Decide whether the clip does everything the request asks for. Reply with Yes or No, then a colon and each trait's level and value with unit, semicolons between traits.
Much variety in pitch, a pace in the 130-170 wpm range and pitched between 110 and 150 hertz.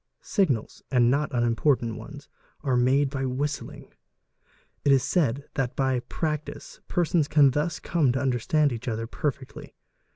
No: average, 3.1 semitones; average, 150 wpm; low, 135 Hz